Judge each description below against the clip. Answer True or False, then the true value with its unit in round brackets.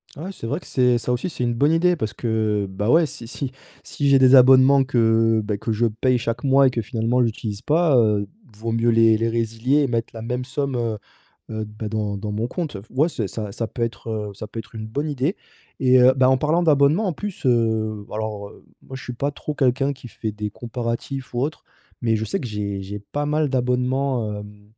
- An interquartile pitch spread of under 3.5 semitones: False (3.8 semitones)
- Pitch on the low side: True (120 Hz)